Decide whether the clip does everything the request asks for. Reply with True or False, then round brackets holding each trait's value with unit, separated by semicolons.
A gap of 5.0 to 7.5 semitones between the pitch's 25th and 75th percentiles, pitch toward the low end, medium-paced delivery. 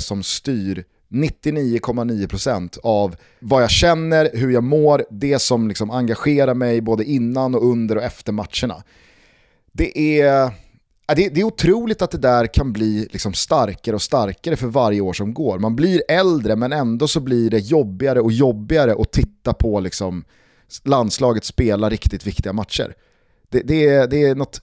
True (5.3 semitones; 120 Hz; 160 wpm)